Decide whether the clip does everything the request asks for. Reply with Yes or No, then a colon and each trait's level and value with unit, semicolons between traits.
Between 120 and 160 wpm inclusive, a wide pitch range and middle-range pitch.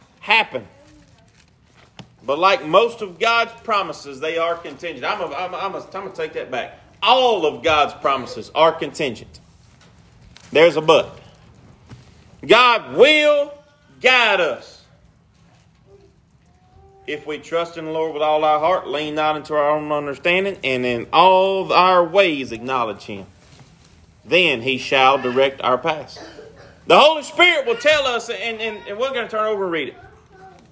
Yes: average, 155 wpm; wide, 8.1 semitones; medium, 165 Hz